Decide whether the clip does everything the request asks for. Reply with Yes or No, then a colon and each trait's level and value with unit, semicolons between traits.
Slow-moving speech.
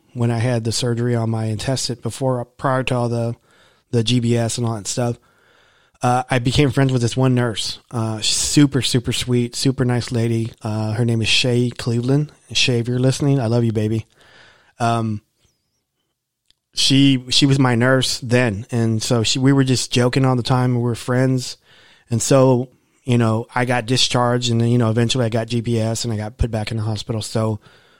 No: average, 195 wpm